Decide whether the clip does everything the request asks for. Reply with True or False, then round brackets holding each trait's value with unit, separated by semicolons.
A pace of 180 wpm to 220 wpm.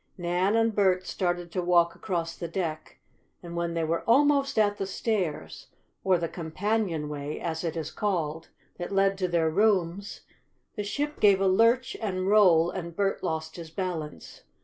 False (170 wpm)